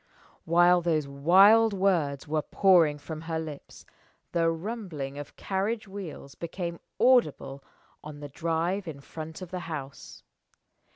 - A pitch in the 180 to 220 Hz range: No, medium, 165 Hz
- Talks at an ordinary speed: No, slow, 130 wpm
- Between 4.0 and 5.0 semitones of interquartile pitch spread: Yes, average, 4.3 semitones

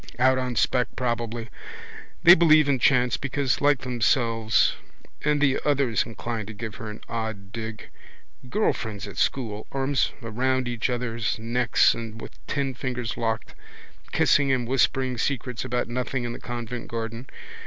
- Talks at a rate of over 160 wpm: No, average, 155 wpm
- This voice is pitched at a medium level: No, low, 120 Hz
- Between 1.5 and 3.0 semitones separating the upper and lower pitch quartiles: Yes, narrow, 2.4 semitones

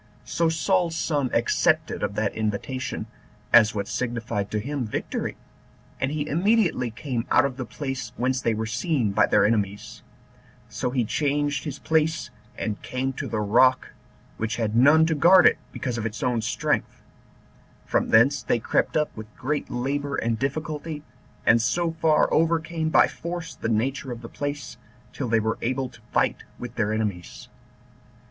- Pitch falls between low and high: No, low, 130 Hz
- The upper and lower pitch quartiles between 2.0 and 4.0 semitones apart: No, average, 5.2 semitones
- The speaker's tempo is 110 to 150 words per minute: No, average, 165 wpm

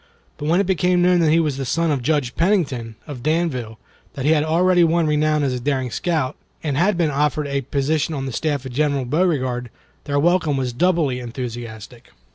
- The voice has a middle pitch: Yes, medium, 150 Hz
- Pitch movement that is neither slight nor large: Yes, average, 4.3 semitones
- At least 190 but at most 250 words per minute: Yes, fast, 205 wpm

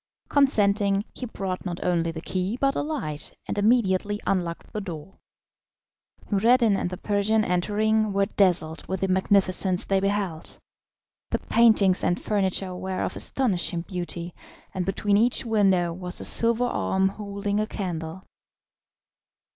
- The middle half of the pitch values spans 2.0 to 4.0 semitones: Yes, average, 2.8 semitones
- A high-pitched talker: Yes, high, 195 Hz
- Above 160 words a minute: No, average, 140 wpm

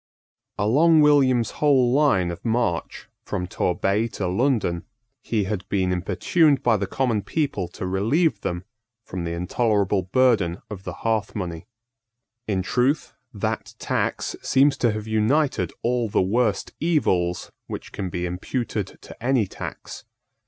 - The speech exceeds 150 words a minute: No, average, 140 wpm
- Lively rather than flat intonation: Yes, wide, 5.7 semitones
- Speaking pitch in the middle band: No, low, 110 Hz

